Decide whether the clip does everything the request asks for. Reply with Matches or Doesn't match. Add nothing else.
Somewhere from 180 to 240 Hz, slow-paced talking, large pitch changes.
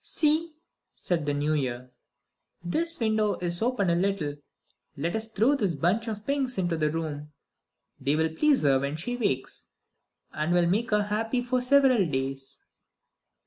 Doesn't match